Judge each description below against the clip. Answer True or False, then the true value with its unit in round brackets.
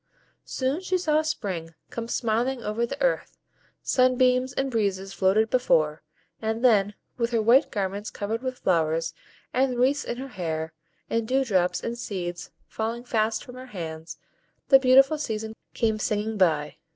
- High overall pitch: True (225 Hz)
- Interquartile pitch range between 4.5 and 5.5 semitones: True (4.8 semitones)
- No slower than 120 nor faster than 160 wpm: True (155 wpm)